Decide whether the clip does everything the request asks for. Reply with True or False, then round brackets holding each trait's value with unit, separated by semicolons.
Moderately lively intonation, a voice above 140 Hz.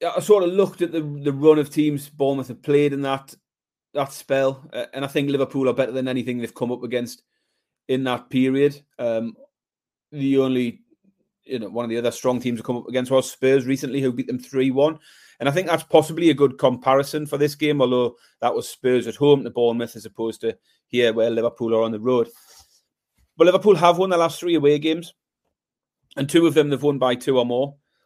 False (3.7 semitones; 135 Hz)